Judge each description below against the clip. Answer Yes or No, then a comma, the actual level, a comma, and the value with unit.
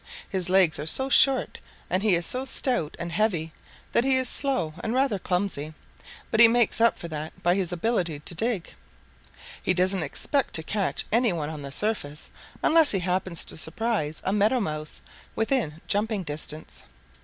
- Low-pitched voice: No, high, 190 Hz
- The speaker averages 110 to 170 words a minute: No, average, 180 wpm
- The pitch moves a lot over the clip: Yes, wide, 6.2 semitones